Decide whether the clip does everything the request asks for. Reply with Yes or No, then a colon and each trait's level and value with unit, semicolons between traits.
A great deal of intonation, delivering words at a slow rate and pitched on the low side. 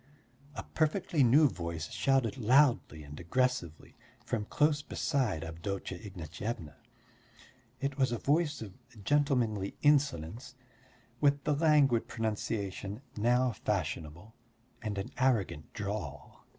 Yes: wide, 6.4 semitones; slow, 110 wpm; low, 115 Hz